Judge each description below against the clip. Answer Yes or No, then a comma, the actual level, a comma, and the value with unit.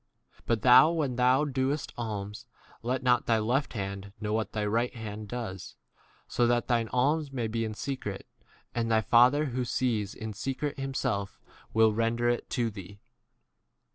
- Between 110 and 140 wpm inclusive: No, average, 170 wpm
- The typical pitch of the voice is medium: No, low, 120 Hz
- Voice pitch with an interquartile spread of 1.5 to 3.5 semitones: Yes, average, 3.0 semitones